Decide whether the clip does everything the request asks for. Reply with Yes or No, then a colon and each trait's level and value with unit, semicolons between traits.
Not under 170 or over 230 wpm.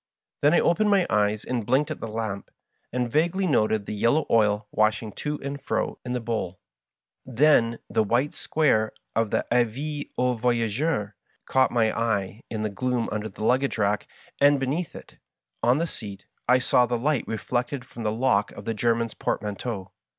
Yes: average, 185 wpm